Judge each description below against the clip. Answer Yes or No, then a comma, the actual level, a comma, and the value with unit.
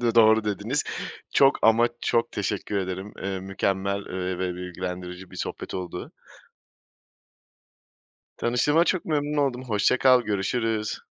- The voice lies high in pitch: No, low, 105 Hz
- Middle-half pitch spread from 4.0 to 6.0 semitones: Yes, average, 4.5 semitones